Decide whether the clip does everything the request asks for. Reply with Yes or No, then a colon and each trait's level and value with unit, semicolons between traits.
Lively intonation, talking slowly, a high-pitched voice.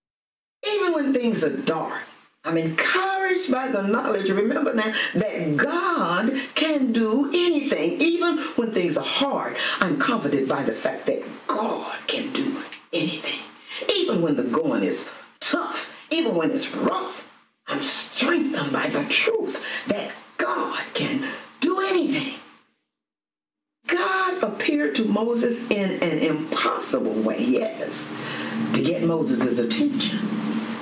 Yes: wide, 7.3 semitones; slow, 125 wpm; very high, 275 Hz